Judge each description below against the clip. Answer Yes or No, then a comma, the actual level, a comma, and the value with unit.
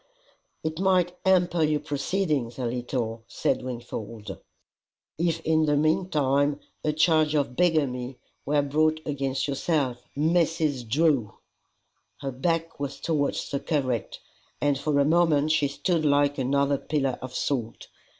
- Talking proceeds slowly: Yes, slow, 130 wpm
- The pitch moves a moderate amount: Yes, average, 3.0 semitones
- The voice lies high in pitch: No, medium, 145 Hz